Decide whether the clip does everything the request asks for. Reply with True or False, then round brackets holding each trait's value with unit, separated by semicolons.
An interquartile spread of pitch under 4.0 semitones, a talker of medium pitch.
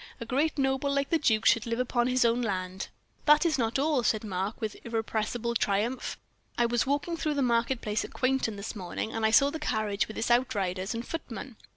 False (3.6 semitones; 235 Hz)